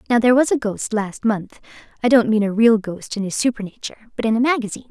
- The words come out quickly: Yes, fast, 220 wpm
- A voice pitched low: No, high, 225 Hz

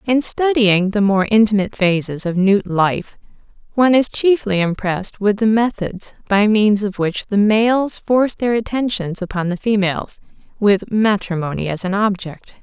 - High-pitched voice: Yes, high, 205 Hz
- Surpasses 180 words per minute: No, average, 155 wpm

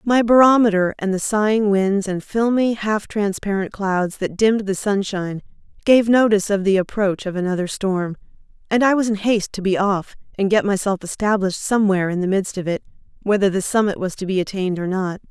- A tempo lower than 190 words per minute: No, average, 195 wpm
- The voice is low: No, high, 200 Hz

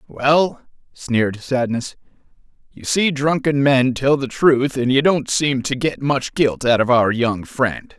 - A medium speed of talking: Yes, average, 175 wpm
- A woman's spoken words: No, male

